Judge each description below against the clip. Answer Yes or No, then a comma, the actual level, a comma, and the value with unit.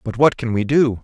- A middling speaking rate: No, fast, 290 wpm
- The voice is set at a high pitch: No, low, 125 Hz